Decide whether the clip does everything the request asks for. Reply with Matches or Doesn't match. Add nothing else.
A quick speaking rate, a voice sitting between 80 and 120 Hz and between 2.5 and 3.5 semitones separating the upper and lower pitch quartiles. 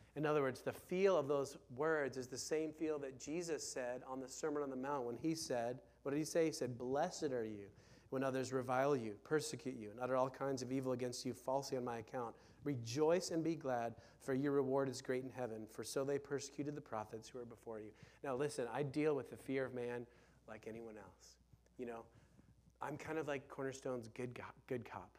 Doesn't match